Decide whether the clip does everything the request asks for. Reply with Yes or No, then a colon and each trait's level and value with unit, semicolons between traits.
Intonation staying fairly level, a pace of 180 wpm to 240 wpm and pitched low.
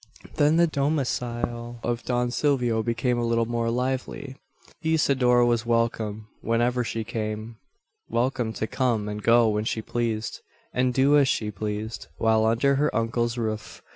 No: narrow, 2.2 semitones; average, 150 wpm; low, 120 Hz